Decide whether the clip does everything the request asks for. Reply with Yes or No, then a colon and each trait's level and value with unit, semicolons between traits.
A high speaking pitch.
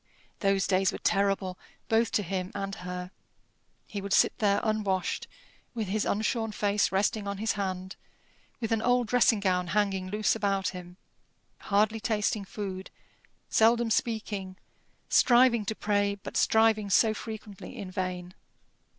Yes: high, 200 Hz